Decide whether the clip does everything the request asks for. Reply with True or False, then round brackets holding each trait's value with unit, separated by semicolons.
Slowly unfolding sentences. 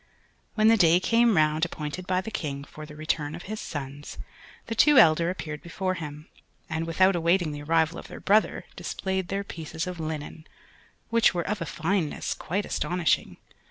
False (180 wpm)